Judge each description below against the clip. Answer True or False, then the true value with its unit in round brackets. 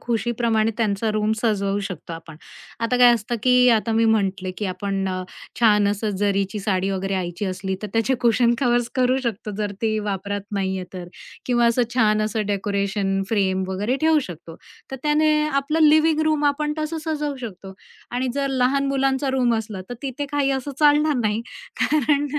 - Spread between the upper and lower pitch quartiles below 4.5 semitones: False (5.1 semitones)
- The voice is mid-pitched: False (225 Hz)